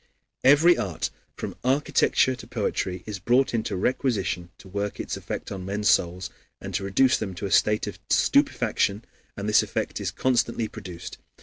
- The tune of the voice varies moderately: Yes, average, 4.6 semitones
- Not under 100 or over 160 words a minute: No, average, 170 wpm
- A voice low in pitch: Yes, low, 105 Hz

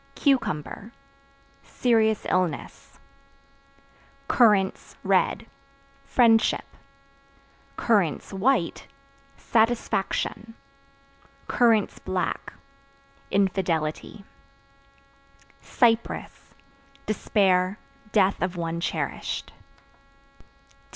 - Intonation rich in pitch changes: No, average, 3.6 semitones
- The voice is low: No, high, 200 Hz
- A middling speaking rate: No, slow, 45 wpm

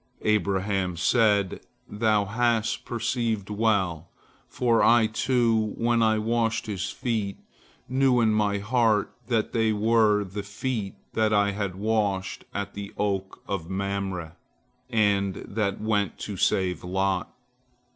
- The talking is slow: Yes, slow, 125 wpm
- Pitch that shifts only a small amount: Yes, narrow, 2.3 semitones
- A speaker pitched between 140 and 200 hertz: No, low, 105 Hz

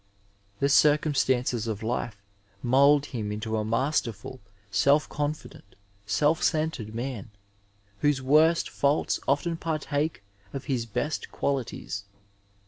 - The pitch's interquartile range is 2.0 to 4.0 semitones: No, average, 4.6 semitones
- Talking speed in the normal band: No, slow, 110 wpm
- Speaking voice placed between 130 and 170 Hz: Yes, low, 135 Hz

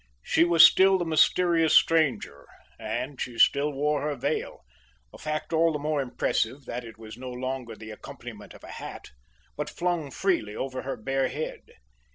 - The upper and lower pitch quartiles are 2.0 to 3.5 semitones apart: No, average, 4.5 semitones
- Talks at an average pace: Yes, average, 175 wpm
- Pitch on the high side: No, medium, 140 Hz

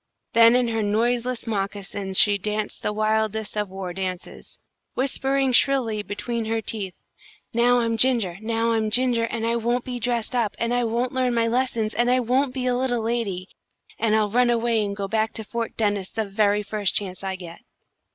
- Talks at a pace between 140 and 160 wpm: No, average, 190 wpm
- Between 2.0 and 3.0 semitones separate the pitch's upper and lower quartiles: Yes, average, 2.7 semitones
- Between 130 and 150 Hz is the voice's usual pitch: No, high, 225 Hz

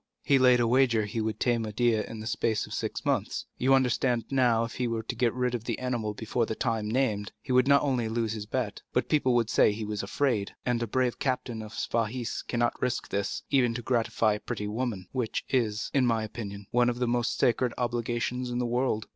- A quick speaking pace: Yes, fast, 230 wpm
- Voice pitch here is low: Yes, low, 120 Hz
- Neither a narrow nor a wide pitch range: No, narrow, 2.3 semitones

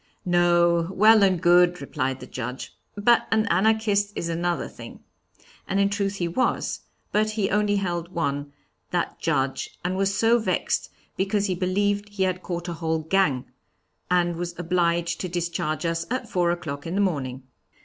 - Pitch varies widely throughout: No, average, 3.0 semitones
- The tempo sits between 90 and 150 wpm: No, average, 170 wpm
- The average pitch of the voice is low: No, medium, 175 Hz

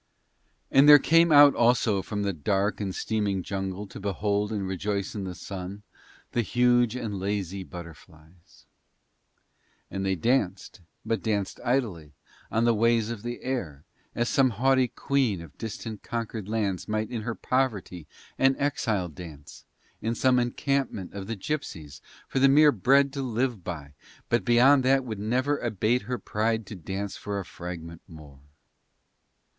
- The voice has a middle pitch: No, low, 105 Hz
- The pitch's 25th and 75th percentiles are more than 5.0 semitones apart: No, average, 4.5 semitones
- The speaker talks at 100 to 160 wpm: Yes, average, 155 wpm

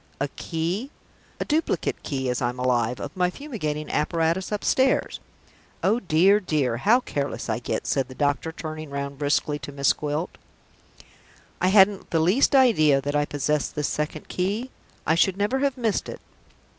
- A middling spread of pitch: No, wide, 5.9 semitones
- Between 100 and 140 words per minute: No, average, 165 wpm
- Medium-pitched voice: Yes, medium, 155 Hz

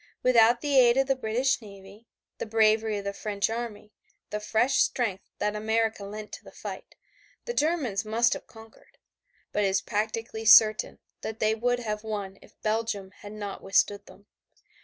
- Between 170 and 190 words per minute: Yes, average, 175 wpm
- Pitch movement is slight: Yes, narrow, 2.0 semitones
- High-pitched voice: Yes, high, 220 Hz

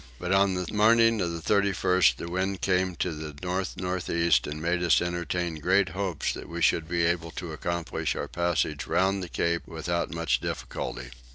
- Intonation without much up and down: Yes, narrow, 1.9 semitones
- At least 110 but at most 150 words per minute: No, average, 190 wpm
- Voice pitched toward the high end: No, very low, 85 Hz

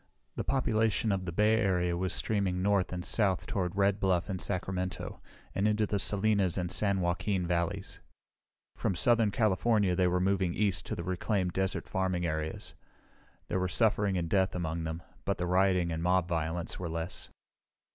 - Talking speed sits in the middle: Yes, average, 175 wpm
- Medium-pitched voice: No, very low, 95 Hz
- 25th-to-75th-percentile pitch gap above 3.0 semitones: No, narrow, 2.4 semitones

